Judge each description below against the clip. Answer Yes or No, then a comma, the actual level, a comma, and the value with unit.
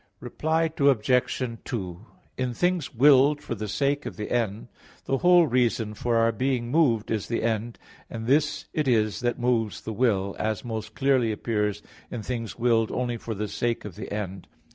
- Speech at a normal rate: Yes, average, 180 wpm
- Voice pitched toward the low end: Yes, low, 115 Hz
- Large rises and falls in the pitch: No, average, 3.3 semitones